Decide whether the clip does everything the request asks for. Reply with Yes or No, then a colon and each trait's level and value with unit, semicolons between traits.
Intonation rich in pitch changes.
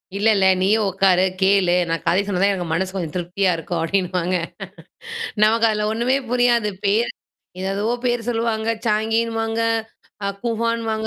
No: average, 3.4 semitones